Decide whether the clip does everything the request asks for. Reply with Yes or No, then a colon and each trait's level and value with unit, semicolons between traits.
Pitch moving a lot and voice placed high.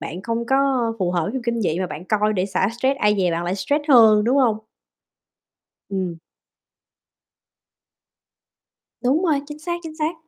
Yes: wide, 6.4 semitones; high, 225 Hz